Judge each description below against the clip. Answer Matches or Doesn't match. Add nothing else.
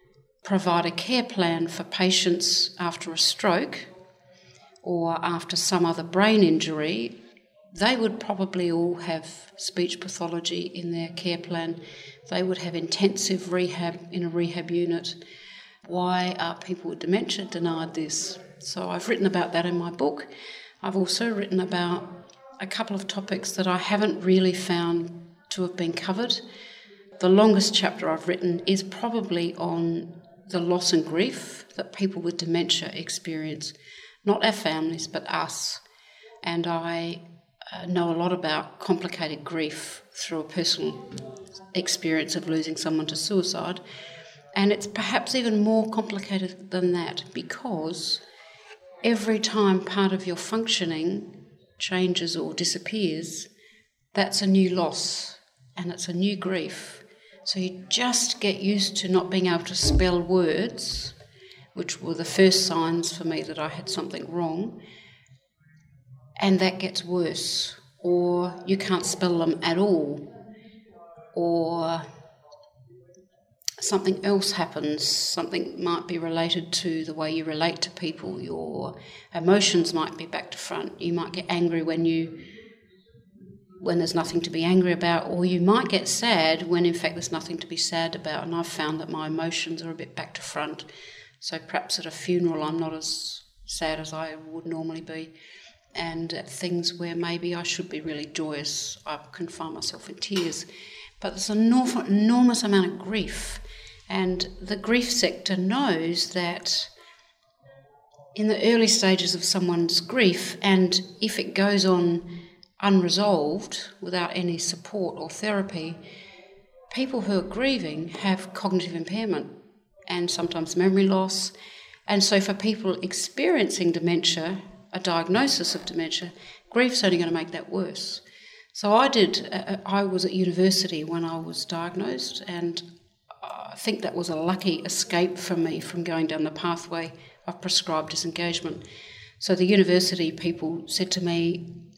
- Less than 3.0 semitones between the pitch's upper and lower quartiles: Matches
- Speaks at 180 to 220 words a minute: Doesn't match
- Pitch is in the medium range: Matches